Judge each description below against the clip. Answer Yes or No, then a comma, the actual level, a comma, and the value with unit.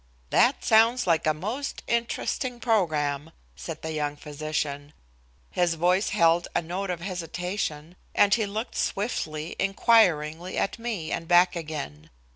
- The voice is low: No, medium, 175 Hz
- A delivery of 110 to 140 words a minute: Yes, slow, 135 wpm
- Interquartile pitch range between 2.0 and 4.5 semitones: No, average, 5.2 semitones